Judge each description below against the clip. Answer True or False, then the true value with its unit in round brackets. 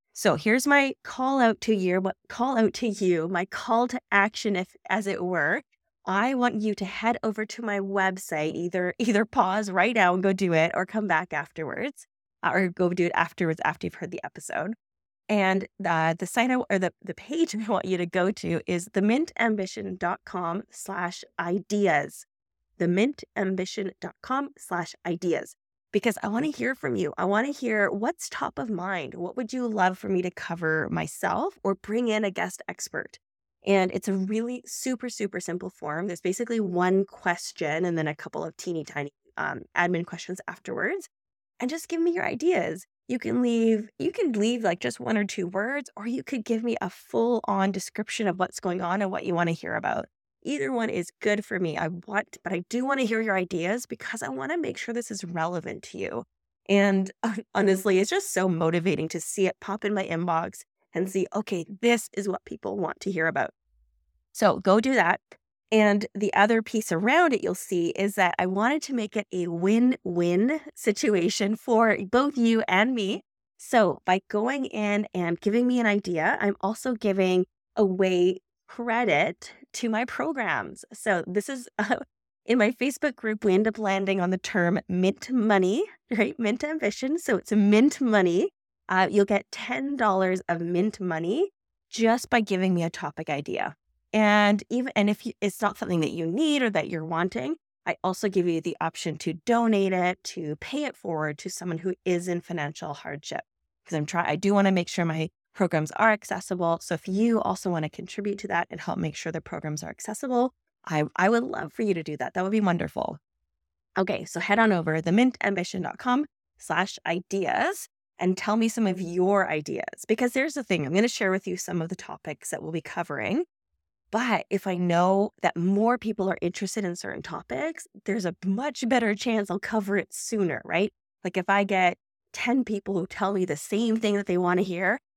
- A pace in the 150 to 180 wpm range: False (200 wpm)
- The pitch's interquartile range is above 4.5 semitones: False (4.2 semitones)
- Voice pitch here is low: False (200 Hz)